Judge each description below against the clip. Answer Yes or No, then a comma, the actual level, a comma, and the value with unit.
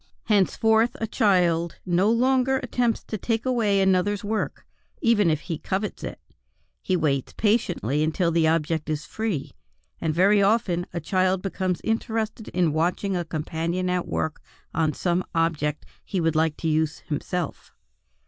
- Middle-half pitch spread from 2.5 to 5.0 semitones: Yes, average, 4.5 semitones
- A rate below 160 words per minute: Yes, average, 150 wpm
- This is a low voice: No, medium, 180 Hz